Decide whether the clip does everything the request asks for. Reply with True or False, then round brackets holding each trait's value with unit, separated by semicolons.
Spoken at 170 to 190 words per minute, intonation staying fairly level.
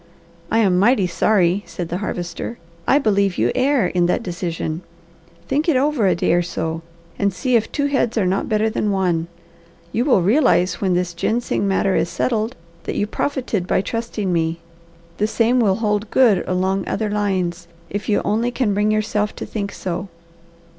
False (180 wpm; 4.0 semitones)